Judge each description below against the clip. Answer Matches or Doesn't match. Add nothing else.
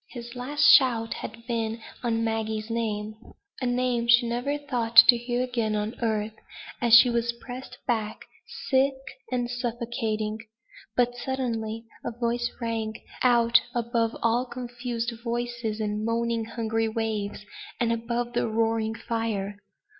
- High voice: Matches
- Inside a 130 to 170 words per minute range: Matches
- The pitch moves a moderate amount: Doesn't match